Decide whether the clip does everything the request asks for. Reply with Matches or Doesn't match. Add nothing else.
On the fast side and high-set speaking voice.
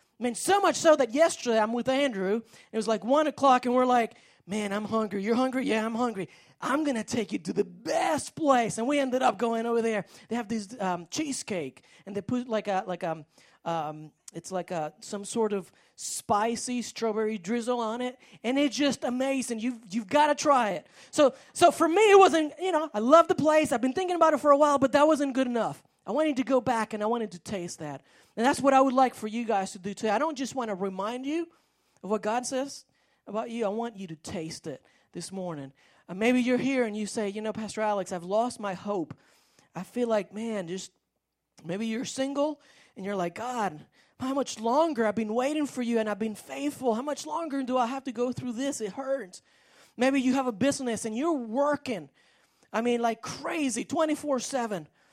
Matches